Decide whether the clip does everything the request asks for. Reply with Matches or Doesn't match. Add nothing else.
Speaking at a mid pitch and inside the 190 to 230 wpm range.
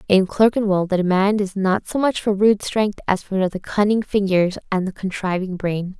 Doesn't match